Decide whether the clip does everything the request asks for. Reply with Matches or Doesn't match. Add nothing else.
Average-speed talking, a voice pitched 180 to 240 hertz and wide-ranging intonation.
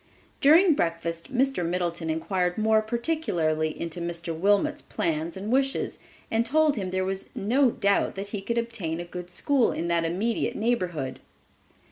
Matches